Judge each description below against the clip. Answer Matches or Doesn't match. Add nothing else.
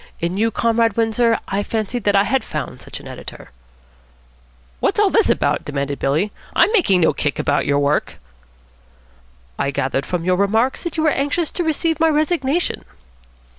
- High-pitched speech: Matches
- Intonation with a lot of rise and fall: Matches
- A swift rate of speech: Doesn't match